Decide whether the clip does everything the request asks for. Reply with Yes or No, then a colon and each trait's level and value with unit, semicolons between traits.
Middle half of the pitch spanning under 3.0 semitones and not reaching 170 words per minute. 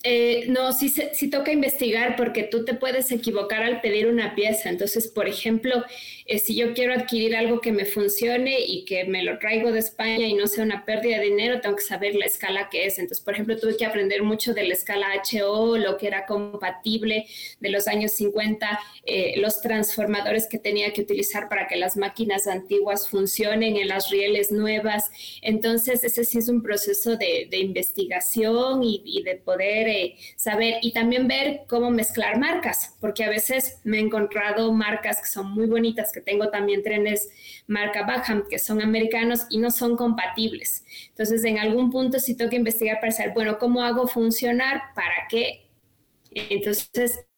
No: narrow, 2.4 semitones; average, 185 wpm